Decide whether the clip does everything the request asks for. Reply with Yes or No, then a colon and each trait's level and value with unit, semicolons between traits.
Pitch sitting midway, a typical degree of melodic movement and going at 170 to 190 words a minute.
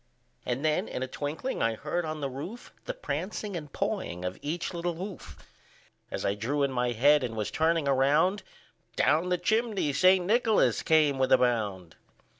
No: medium, 150 Hz; wide, 6.2 semitones; average, 180 wpm